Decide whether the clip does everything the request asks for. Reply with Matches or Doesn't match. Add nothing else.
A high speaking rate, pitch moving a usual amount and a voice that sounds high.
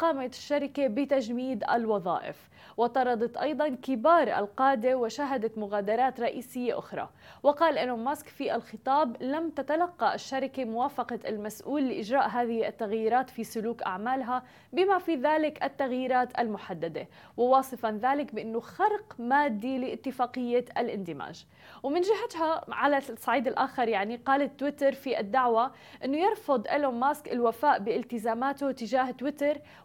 Doesn't match